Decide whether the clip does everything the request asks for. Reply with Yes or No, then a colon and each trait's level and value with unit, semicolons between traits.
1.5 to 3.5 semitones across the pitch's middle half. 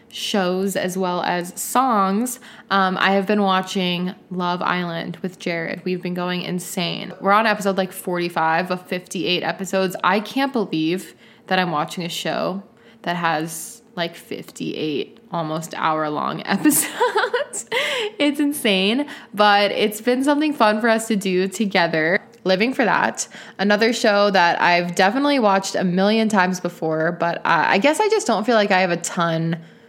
No: average, 4.1 semitones